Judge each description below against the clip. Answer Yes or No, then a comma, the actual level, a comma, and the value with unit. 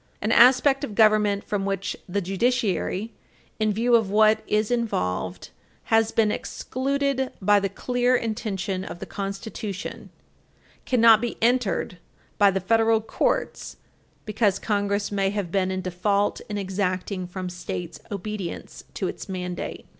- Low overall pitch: No, high, 205 Hz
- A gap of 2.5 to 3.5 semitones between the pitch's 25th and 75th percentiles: Yes, average, 2.8 semitones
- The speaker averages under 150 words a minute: Yes, average, 140 wpm